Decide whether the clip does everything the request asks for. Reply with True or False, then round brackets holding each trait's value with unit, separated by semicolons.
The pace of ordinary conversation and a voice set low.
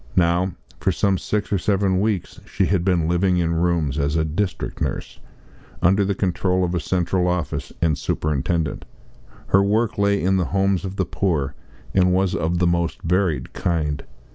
True (175 wpm; 90 Hz)